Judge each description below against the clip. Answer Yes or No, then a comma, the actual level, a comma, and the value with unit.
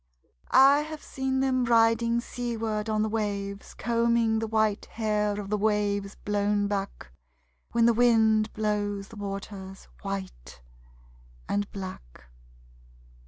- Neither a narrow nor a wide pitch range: No, narrow, 2.3 semitones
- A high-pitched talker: Yes, high, 215 Hz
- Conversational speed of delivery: No, slow, 120 wpm